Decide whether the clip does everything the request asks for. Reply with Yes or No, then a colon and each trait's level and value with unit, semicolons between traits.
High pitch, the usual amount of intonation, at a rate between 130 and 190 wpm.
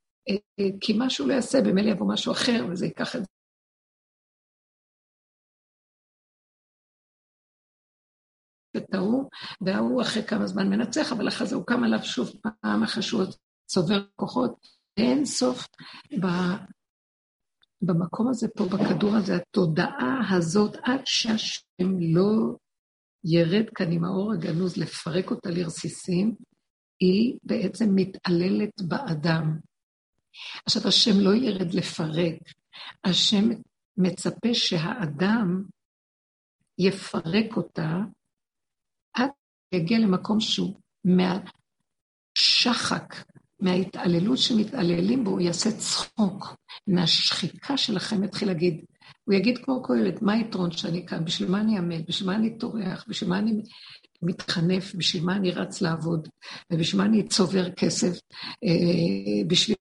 No: high, 195 Hz; average, 3.5 semitones; average, 110 wpm